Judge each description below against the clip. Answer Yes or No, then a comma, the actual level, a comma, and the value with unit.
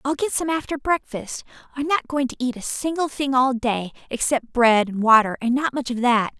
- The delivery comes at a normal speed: No, fast, 215 wpm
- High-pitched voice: Yes, very high, 260 Hz